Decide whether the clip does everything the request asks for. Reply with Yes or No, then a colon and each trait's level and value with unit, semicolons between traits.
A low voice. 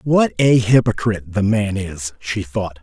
Yes: low, 105 Hz